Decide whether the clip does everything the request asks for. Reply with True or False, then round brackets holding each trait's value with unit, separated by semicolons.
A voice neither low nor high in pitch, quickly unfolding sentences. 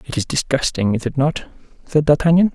False (165 Hz; 190 wpm)